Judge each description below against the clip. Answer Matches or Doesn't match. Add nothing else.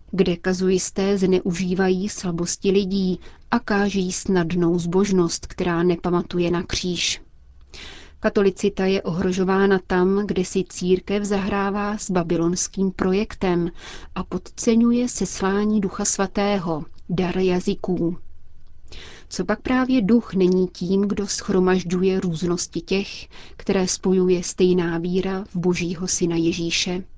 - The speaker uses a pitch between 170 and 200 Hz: Matches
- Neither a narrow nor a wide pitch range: Doesn't match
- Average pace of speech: Doesn't match